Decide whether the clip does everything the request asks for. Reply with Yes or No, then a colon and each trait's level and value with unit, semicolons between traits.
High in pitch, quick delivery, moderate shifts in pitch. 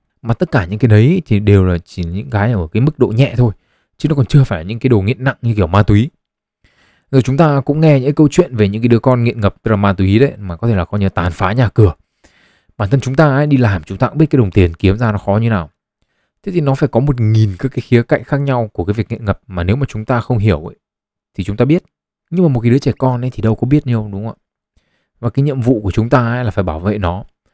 No: low, 115 Hz; fast, 305 wpm; average, 5.0 semitones